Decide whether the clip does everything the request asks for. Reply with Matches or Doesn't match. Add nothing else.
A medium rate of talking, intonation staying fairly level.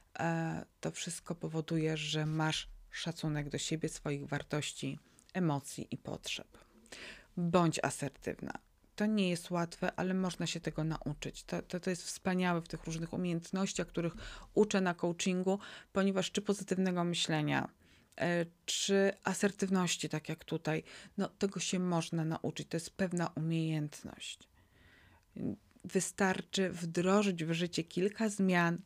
Doesn't match